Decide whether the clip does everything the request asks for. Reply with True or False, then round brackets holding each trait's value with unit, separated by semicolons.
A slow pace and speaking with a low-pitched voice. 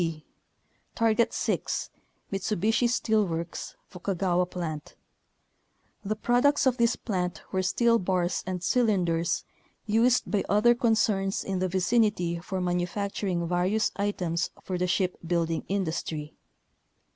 False (120 wpm; 190 Hz)